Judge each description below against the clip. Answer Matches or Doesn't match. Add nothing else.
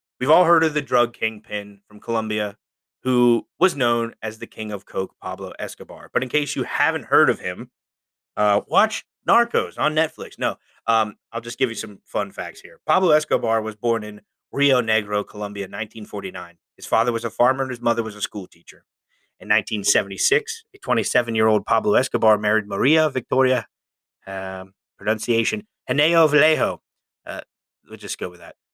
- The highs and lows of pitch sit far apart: Doesn't match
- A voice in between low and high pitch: Doesn't match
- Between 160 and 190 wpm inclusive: Matches